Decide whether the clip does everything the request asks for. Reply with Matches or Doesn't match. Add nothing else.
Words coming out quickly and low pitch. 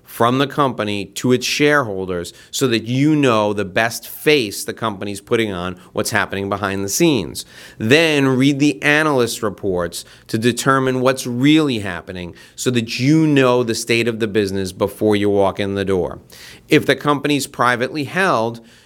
Doesn't match